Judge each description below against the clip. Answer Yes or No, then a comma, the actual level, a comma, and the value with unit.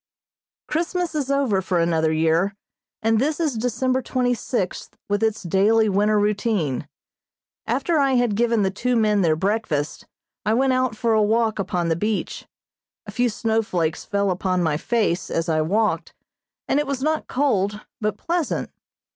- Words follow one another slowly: No, average, 165 wpm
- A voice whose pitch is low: No, high, 215 Hz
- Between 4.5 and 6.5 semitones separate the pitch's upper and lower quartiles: Yes, average, 4.8 semitones